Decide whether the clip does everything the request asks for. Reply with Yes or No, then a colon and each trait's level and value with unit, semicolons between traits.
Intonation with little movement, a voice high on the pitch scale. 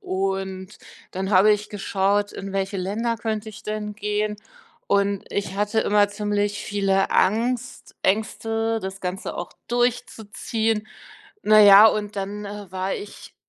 Yes: narrow, 1.7 semitones; high, 205 Hz